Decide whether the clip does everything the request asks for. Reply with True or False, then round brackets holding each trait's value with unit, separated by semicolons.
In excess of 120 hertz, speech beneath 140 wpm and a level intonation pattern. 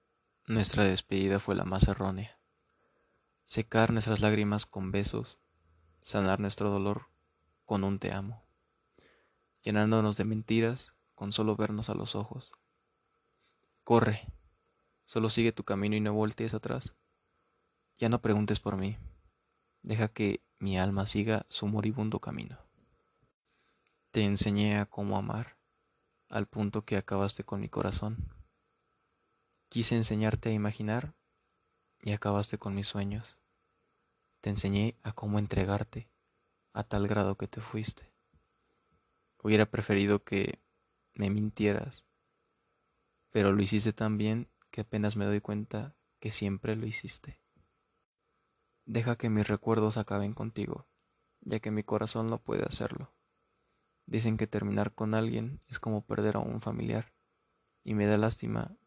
False (105 Hz; 130 wpm; 1.6 semitones)